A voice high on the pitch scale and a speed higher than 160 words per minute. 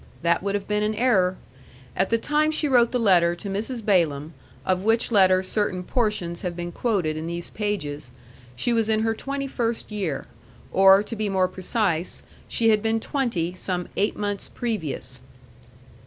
Yes: high, 200 Hz; average, 175 wpm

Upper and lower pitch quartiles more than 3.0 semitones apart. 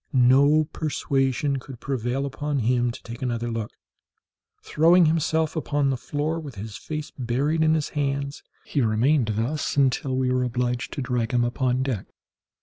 Yes: average, 3.4 semitones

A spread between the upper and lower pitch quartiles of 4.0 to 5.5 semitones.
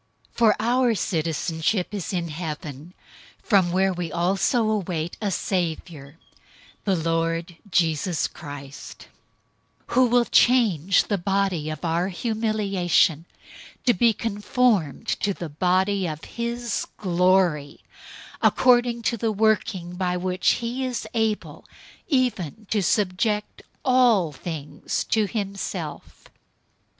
Yes: average, 4.8 semitones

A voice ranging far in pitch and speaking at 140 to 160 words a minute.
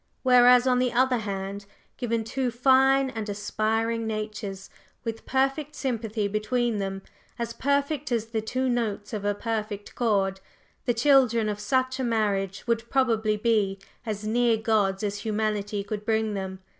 No: average, 3.1 semitones; average, 155 wpm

